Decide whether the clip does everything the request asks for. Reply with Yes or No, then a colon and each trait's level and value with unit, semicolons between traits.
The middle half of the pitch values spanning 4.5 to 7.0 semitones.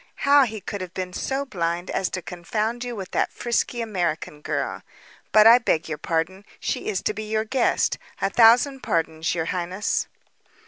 Yes: average, 4.9 semitones